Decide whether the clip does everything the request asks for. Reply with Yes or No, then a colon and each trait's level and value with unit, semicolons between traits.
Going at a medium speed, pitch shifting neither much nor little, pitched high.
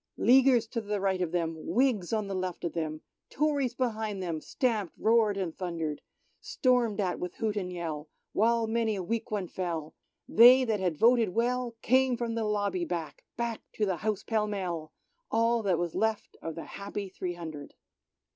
Yes: average, 185 wpm; average, 4.8 semitones; high, 205 Hz